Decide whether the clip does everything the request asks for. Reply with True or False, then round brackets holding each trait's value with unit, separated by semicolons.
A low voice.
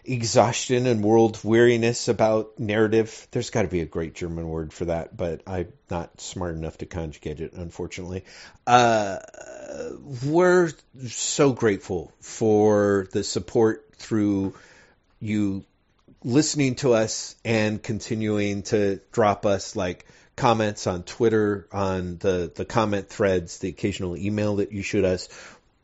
True (105 Hz)